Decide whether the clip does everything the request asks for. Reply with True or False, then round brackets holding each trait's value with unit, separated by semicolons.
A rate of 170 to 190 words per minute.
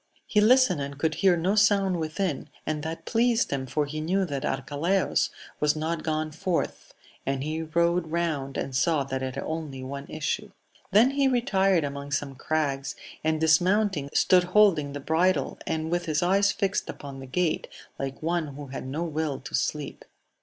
True (180 wpm)